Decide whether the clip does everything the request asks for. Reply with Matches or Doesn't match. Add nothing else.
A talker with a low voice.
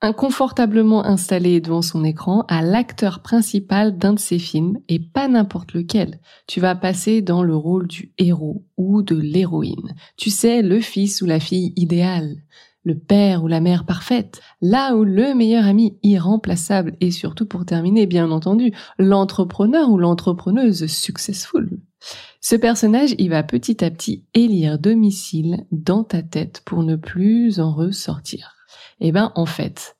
Doesn't match